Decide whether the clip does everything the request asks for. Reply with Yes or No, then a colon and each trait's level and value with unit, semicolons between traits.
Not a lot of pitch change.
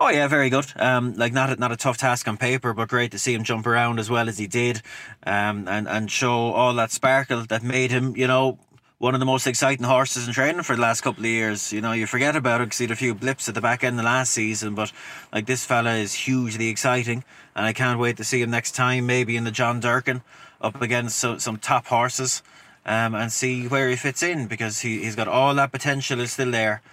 Yes: narrow, 2.1 semitones